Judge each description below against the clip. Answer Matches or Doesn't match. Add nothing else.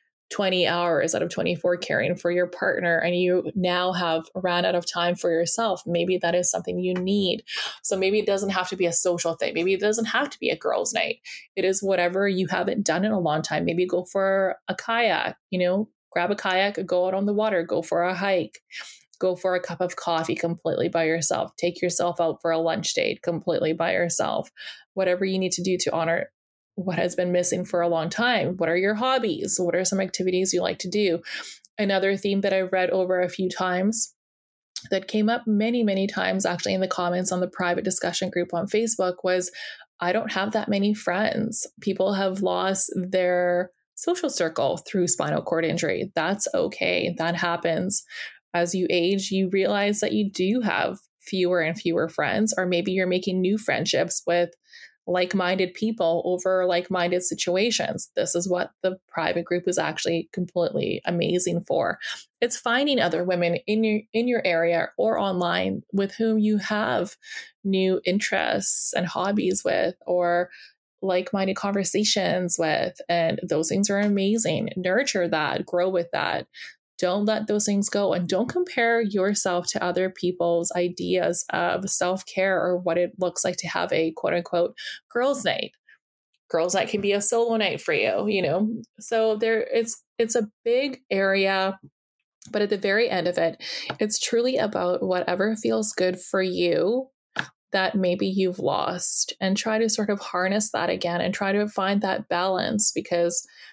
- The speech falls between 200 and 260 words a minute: Doesn't match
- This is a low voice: Doesn't match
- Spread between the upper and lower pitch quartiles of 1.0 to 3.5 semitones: Matches